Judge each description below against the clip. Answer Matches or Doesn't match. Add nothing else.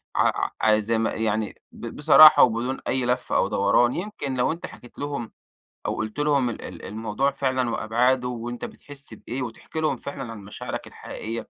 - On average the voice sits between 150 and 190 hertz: Doesn't match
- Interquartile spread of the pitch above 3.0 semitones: Matches